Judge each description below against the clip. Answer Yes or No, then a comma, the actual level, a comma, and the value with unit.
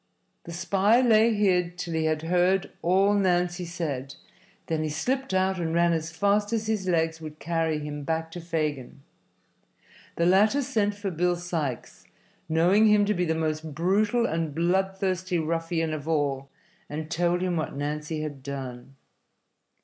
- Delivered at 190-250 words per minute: No, average, 160 wpm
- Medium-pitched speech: Yes, medium, 170 Hz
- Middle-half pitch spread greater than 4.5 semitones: No, average, 3.4 semitones